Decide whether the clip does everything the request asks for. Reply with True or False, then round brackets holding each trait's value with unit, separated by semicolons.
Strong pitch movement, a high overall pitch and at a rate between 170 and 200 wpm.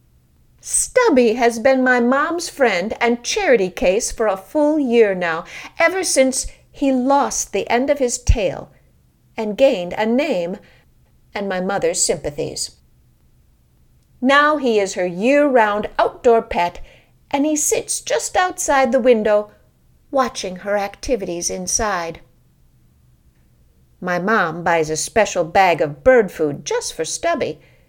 False (6.8 semitones; 235 Hz; 135 wpm)